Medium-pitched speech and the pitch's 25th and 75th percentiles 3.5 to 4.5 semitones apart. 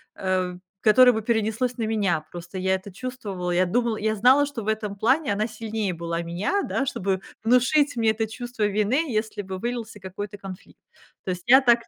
No: high, 215 Hz; average, 4.2 semitones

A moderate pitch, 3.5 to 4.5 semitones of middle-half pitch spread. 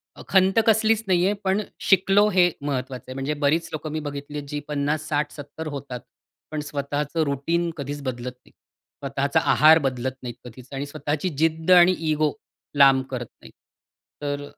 No: medium, 145 Hz; average, 3.1 semitones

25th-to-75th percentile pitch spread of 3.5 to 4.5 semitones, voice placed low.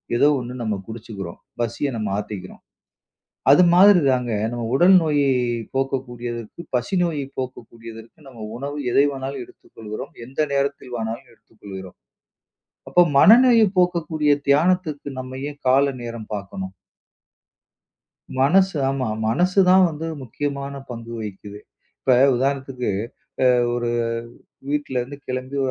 Yes: average, 3.9 semitones; low, 130 Hz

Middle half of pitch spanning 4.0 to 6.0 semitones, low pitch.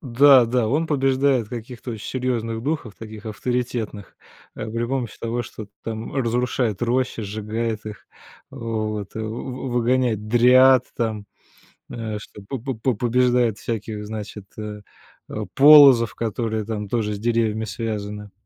No: narrow, 2.6 semitones; low, 115 Hz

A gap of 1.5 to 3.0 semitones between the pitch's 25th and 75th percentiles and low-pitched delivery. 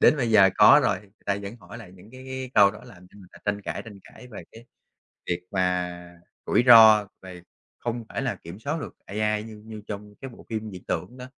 No: average, 3.5 semitones; low, 105 Hz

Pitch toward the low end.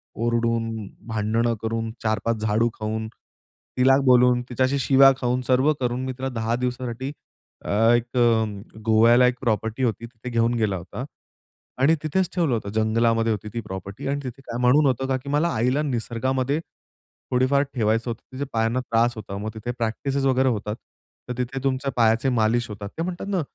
Yes: low, 120 Hz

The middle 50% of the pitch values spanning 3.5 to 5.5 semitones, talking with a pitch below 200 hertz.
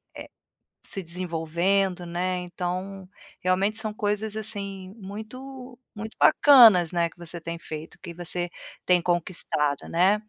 No: average, 3.1 semitones; medium, 185 Hz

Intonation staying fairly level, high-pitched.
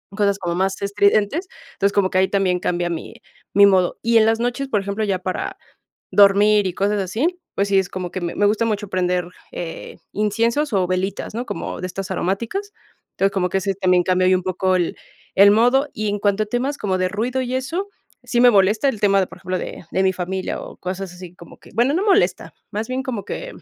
No: average, 3.4 semitones; high, 200 Hz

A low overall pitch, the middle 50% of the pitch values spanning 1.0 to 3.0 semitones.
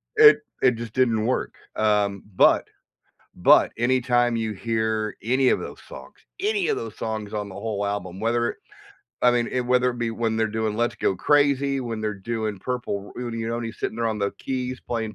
Yes: low, 115 Hz; narrow, 2.6 semitones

